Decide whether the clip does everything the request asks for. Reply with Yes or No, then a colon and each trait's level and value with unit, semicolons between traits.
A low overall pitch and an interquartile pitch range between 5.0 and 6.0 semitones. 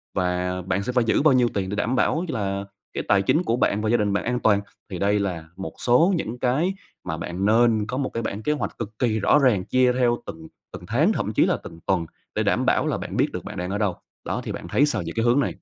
No: low, 110 Hz; average, 4.3 semitones